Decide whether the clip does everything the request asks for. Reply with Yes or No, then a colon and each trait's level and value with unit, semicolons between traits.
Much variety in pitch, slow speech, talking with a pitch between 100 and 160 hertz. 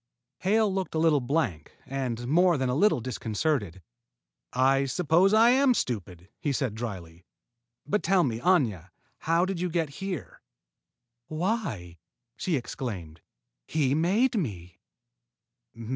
Yes: wide, 8.2 semitones; slow, 130 wpm; medium, 140 Hz